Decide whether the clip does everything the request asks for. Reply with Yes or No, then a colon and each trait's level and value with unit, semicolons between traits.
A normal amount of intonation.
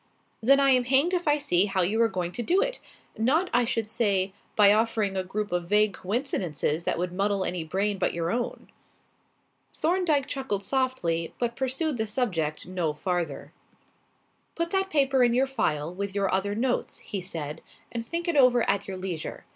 No: wide, 6.2 semitones